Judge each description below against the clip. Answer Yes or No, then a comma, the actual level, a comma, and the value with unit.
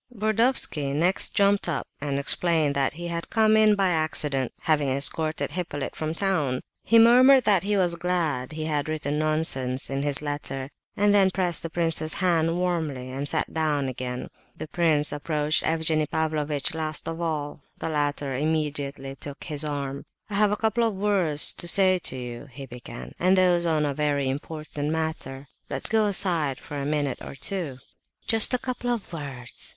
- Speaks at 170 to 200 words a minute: Yes, average, 175 wpm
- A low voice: No, medium, 155 Hz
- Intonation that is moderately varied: Yes, average, 4.1 semitones